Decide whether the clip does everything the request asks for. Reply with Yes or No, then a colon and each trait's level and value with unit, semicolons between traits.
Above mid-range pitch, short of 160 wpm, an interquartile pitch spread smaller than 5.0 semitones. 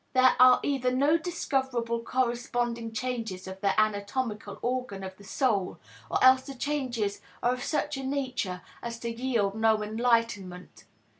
Yes: high, 235 Hz; average, 150 wpm; average, 3.5 semitones